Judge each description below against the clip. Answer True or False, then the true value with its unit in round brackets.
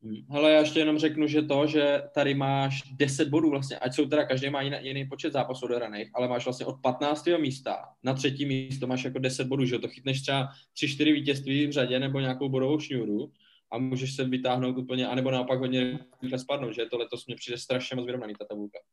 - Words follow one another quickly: True (220 wpm)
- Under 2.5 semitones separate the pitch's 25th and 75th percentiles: True (2.0 semitones)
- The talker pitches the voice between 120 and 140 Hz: True (130 Hz)